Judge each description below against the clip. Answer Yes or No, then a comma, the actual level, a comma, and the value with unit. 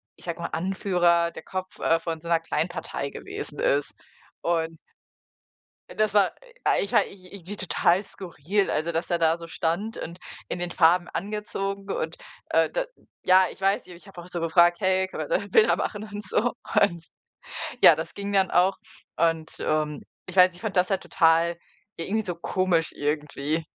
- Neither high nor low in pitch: Yes, medium, 175 Hz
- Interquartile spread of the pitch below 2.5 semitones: No, average, 2.8 semitones